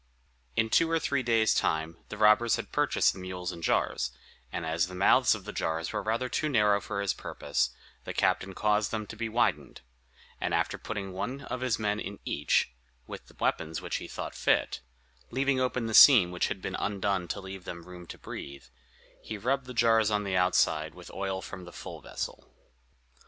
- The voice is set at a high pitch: No, low, 100 Hz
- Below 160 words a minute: No, fast, 205 wpm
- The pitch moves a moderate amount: Yes, average, 4.1 semitones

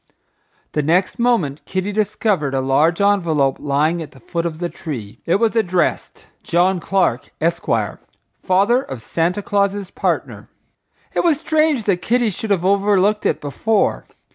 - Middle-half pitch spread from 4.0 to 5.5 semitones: Yes, average, 4.7 semitones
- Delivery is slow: No, average, 150 wpm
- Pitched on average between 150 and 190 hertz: Yes, medium, 185 Hz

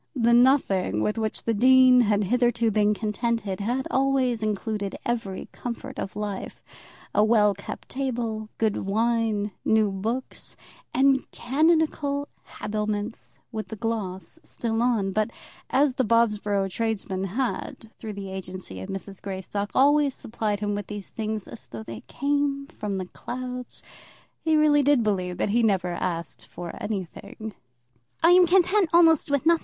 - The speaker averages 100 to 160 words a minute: Yes, average, 150 wpm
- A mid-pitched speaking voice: No, high, 220 Hz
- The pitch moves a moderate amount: Yes, average, 4.2 semitones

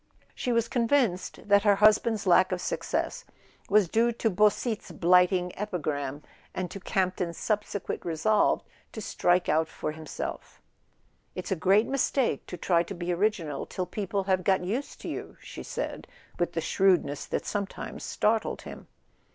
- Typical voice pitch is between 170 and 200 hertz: Yes, high, 190 Hz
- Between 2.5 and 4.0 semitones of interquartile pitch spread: Yes, average, 3.4 semitones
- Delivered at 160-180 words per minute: Yes, average, 165 wpm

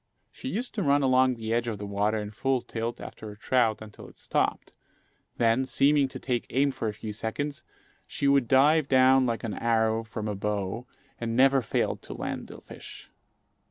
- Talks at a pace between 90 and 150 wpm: No, average, 195 wpm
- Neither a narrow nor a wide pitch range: Yes, average, 3.4 semitones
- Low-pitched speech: Yes, low, 120 Hz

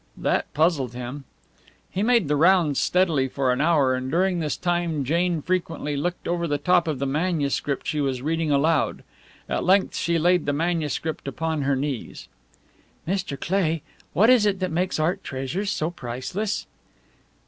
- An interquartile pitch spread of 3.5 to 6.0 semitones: Yes, average, 4.1 semitones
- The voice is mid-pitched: Yes, medium, 160 Hz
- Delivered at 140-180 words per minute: Yes, average, 165 wpm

